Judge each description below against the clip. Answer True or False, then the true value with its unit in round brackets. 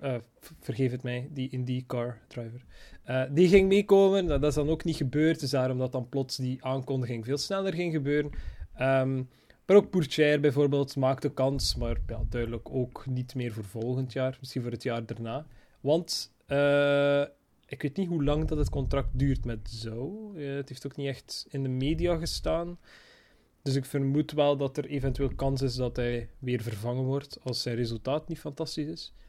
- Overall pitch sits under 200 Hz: True (135 Hz)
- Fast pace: False (190 wpm)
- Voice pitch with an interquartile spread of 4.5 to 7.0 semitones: False (2.9 semitones)